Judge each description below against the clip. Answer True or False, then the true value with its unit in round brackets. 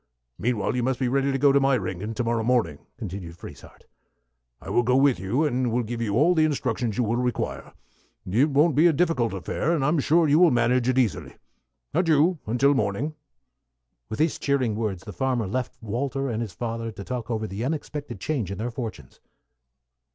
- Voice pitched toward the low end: True (125 Hz)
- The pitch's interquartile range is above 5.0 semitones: False (4.1 semitones)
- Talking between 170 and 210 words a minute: True (195 wpm)